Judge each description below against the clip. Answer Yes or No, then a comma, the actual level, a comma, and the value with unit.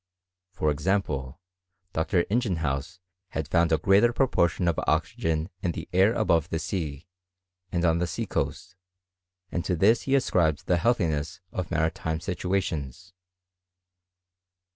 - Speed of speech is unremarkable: No, slow, 130 wpm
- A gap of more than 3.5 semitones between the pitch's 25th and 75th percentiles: No, average, 3.2 semitones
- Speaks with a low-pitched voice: Yes, very low, 85 Hz